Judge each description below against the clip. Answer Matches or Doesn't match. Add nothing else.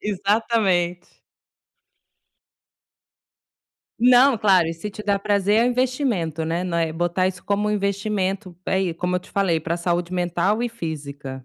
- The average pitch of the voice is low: Doesn't match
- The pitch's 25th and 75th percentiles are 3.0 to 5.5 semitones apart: Matches